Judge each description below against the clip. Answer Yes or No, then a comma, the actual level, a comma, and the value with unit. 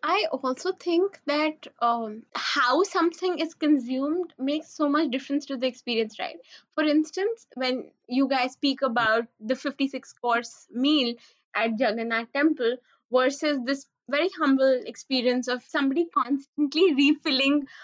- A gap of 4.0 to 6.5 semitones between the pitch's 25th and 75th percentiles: No, average, 3.4 semitones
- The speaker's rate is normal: No, slow, 130 wpm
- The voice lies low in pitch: No, very high, 275 Hz